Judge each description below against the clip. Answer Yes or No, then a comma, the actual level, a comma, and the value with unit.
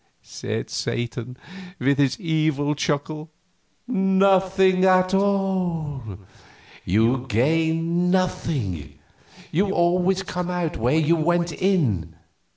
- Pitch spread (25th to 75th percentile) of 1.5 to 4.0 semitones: No, average, 5.3 semitones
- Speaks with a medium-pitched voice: Yes, medium, 165 Hz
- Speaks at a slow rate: Yes, slow, 95 wpm